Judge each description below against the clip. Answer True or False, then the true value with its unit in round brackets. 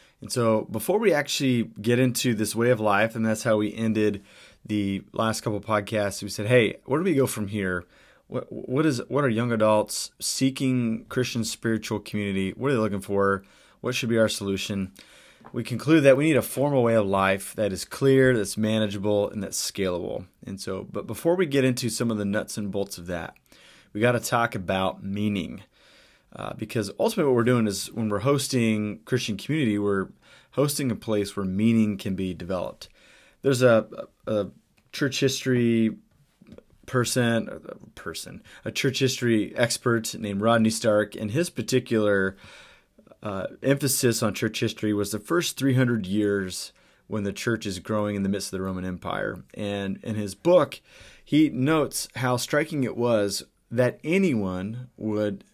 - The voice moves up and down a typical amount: True (3.7 semitones)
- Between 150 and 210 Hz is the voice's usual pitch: False (110 Hz)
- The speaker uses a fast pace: False (175 wpm)